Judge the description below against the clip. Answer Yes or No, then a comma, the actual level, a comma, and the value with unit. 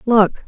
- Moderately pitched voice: No, high, 215 Hz